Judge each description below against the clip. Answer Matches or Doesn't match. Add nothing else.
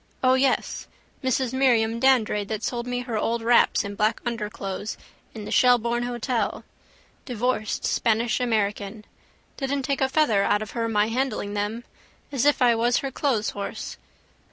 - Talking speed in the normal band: Matches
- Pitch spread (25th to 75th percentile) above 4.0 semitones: Doesn't match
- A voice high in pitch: Matches